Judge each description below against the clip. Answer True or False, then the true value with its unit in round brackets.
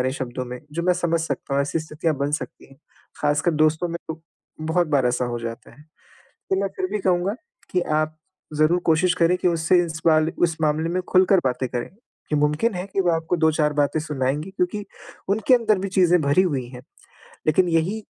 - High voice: False (160 Hz)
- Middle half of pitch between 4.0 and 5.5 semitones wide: False (3.5 semitones)